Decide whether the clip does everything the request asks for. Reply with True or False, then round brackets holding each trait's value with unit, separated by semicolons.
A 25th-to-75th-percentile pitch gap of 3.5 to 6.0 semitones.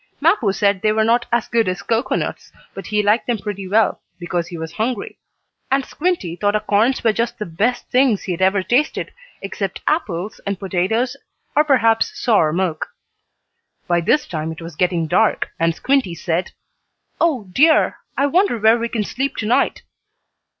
True (5.0 semitones)